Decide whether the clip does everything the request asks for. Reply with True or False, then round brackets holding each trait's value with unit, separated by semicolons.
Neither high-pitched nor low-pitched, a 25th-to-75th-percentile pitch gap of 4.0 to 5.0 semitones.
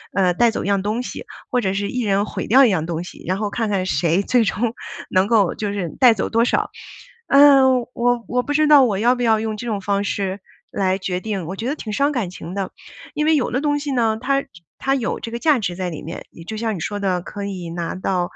False (210 Hz; 4.4 semitones)